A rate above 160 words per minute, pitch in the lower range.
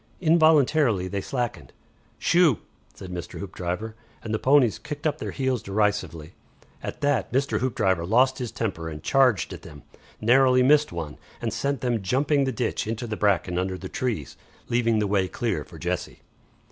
Yes: average, 170 wpm; low, 115 Hz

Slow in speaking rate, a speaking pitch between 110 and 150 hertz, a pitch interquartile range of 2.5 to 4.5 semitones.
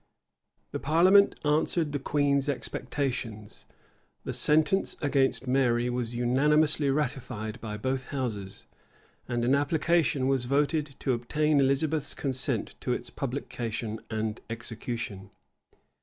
Yes: slow, 115 wpm; low, 135 Hz; average, 3.8 semitones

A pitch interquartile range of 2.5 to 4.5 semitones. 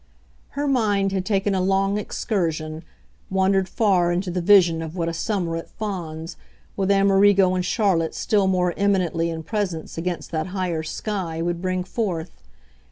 Yes: average, 2.9 semitones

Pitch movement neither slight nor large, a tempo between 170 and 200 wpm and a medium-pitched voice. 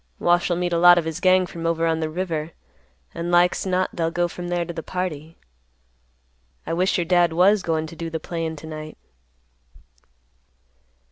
No: narrow, 1.5 semitones; average, 185 wpm; medium, 170 Hz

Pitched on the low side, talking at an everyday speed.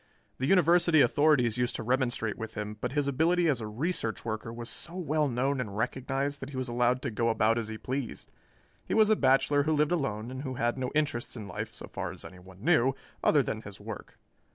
No: low, 130 Hz; fast, 225 wpm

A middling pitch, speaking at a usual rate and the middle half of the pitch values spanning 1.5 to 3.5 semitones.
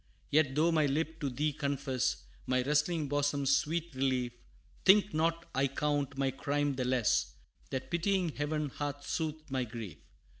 Yes: medium, 145 Hz; average, 155 wpm; average, 2.8 semitones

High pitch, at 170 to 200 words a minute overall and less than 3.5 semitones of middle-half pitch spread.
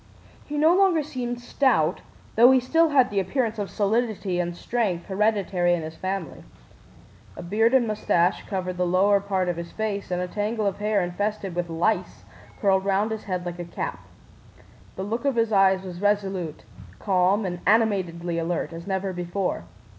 No: high, 195 Hz; average, 175 wpm; average, 3.8 semitones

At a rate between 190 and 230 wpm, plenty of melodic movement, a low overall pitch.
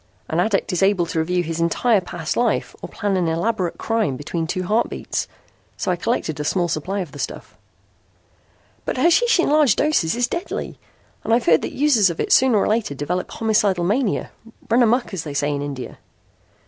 No: average, 195 wpm; wide, 5.8 semitones; high, 190 Hz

